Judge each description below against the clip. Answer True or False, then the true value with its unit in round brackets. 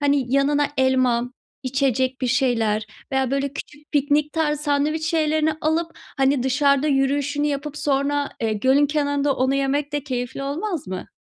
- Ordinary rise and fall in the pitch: False (2.0 semitones)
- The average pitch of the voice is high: True (280 Hz)